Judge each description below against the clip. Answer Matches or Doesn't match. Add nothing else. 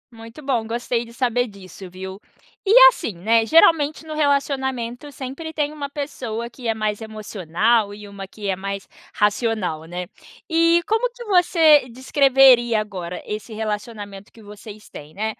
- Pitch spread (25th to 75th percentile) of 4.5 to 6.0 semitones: Matches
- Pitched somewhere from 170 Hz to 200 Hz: Doesn't match